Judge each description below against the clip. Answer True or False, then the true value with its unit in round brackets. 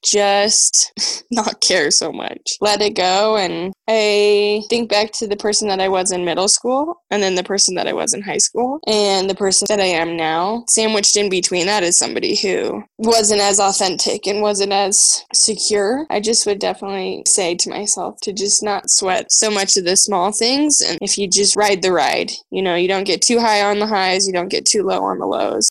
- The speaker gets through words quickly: True (220 wpm)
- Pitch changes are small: True (1.8 semitones)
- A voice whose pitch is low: False (200 Hz)